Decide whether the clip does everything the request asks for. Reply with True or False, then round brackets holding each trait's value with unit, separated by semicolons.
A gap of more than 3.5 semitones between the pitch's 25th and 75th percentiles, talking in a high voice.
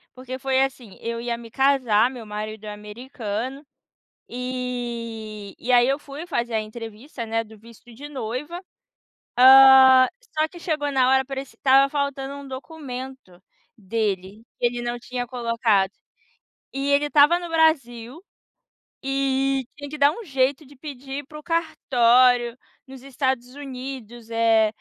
False (2.9 semitones; 255 Hz)